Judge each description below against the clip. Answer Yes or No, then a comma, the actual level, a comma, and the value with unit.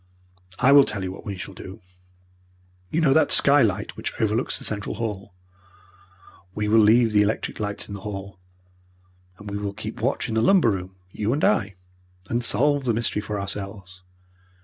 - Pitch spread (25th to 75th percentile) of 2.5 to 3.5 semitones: Yes, average, 2.8 semitones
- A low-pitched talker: Yes, low, 105 Hz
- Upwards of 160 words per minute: Yes, average, 180 wpm